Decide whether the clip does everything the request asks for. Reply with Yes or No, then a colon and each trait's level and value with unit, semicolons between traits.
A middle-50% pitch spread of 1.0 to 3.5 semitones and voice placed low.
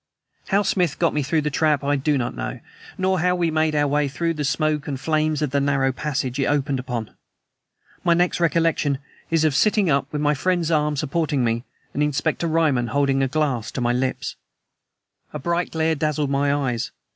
No: average, 2.8 semitones; medium, 150 Hz